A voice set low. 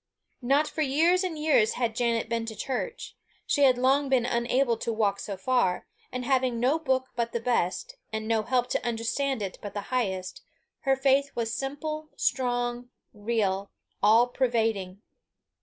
No: high, 245 Hz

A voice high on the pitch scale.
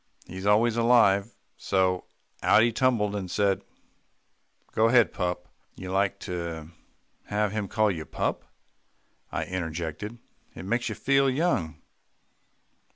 No: low, 100 Hz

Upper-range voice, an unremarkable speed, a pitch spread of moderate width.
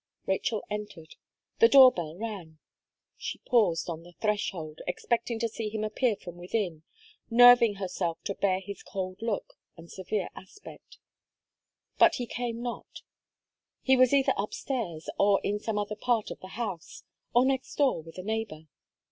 Yes: high, 210 Hz; average, 160 wpm; average, 4.6 semitones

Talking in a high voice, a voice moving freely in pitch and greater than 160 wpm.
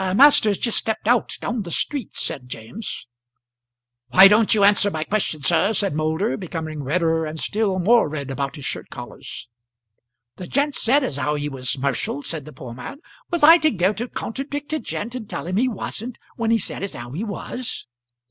Yes: high, 195 Hz; wide, 7.2 semitones; average, 195 wpm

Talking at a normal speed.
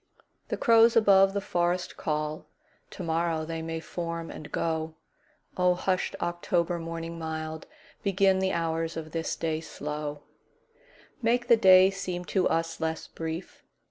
No: slow, 125 wpm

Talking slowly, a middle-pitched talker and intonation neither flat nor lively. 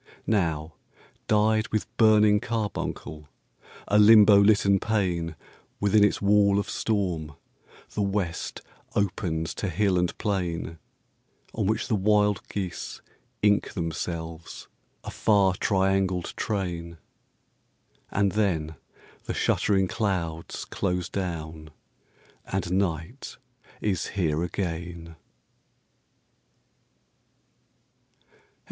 No: slow, 90 wpm; very low, 95 Hz; average, 3.6 semitones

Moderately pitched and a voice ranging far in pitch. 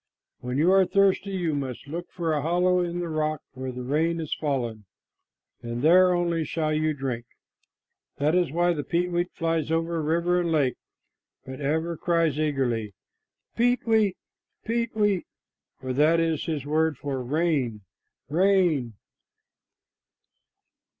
No: medium, 160 Hz; average, 3.8 semitones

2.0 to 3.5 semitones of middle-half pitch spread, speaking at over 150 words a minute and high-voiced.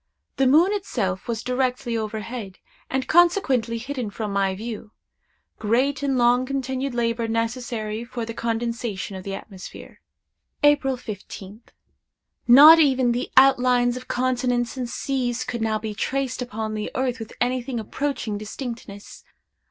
No: average, 2.9 semitones; slow, 135 wpm; high, 240 Hz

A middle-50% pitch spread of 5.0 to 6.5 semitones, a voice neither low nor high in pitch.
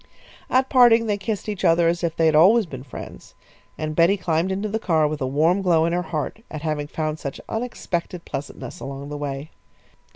No: average, 4.6 semitones; medium, 165 Hz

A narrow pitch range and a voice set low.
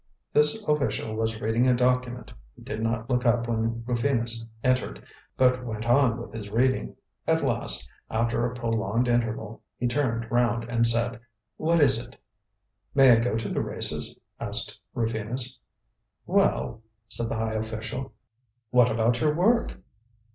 Yes: narrow, 1.9 semitones; low, 115 Hz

